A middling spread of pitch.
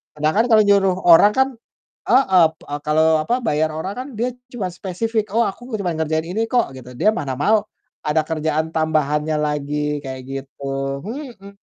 No: wide, 6.0 semitones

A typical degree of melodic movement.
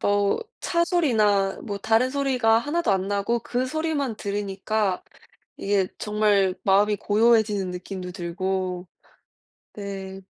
Yes: average, 3.4 semitones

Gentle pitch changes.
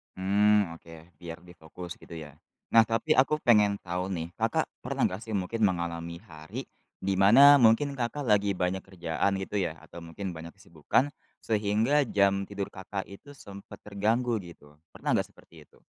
No: average, 3.6 semitones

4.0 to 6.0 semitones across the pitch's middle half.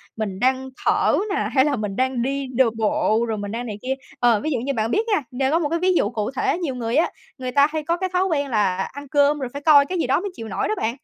Yes: average, 4.7 semitones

